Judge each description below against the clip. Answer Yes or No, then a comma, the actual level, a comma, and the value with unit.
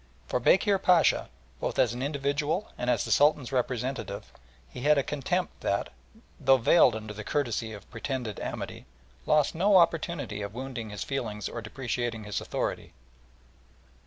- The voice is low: Yes, low, 130 Hz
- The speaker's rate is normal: Yes, average, 155 wpm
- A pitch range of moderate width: Yes, average, 4.8 semitones